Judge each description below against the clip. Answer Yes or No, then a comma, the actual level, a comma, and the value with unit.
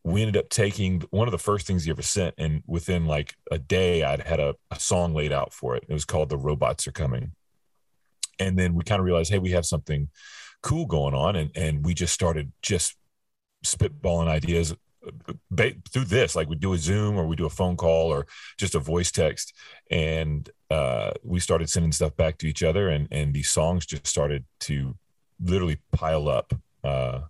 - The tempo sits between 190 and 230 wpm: Yes, fast, 205 wpm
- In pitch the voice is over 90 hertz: No, very low, 80 Hz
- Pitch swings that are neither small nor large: Yes, average, 3.1 semitones